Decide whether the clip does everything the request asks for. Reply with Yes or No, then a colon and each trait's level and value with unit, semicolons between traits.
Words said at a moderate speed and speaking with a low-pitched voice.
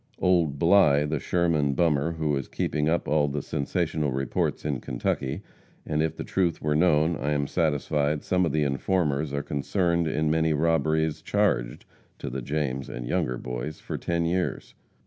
Yes: average, 170 wpm; very low, 75 Hz